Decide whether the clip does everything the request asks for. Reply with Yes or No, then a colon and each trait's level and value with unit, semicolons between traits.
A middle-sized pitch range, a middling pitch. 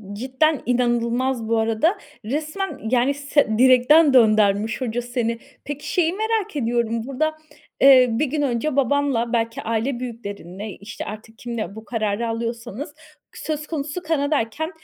No: average, 4.2 semitones; high, 245 Hz